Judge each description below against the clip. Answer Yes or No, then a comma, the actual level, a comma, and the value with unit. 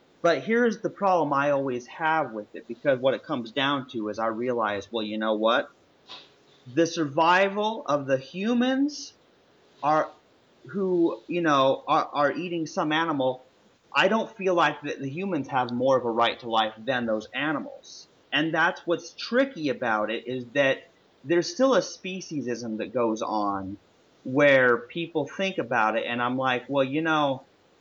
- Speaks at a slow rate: No, average, 170 wpm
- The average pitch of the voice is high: No, medium, 140 Hz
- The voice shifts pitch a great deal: Yes, wide, 5.9 semitones